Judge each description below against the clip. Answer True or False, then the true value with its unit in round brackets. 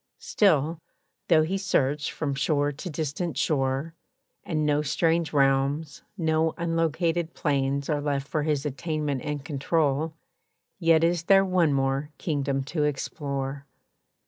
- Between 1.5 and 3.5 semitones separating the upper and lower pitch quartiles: True (2.8 semitones)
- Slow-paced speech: True (130 wpm)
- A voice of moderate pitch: True (150 Hz)